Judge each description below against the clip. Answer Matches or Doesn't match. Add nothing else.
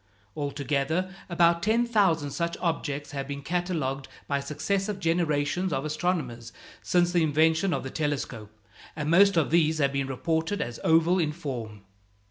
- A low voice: Doesn't match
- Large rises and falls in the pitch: Doesn't match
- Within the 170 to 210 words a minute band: Doesn't match